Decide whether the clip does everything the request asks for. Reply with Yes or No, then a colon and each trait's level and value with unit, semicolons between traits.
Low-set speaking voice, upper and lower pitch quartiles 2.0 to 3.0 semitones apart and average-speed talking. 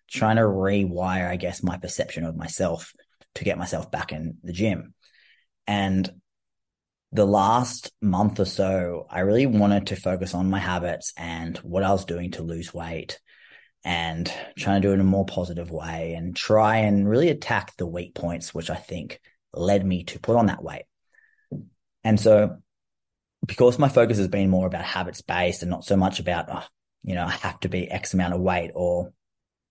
Yes: very low, 95 Hz; narrow, 2.4 semitones; average, 190 wpm